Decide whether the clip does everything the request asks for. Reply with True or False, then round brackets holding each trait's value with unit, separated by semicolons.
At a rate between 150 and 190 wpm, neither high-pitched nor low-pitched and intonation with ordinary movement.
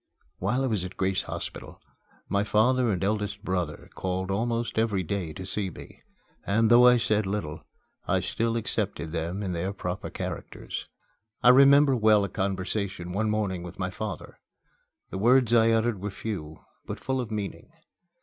False (170 wpm; 105 Hz; 3.4 semitones)